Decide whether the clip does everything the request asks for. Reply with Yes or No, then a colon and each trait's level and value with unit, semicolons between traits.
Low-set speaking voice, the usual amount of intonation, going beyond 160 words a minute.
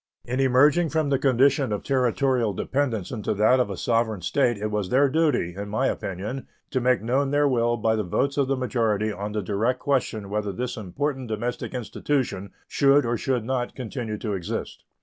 Yes: low, 120 Hz; average, 4.1 semitones; average, 190 wpm